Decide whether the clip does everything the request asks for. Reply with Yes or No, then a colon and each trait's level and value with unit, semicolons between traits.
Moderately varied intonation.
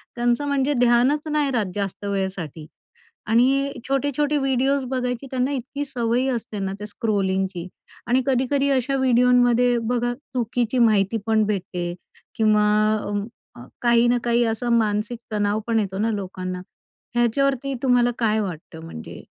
Yes: average, 3.9 semitones